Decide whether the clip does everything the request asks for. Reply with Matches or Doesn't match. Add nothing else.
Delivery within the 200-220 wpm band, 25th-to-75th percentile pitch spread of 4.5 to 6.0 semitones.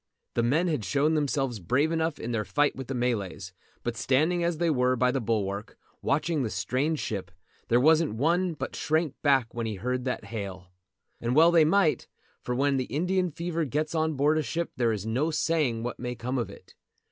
Matches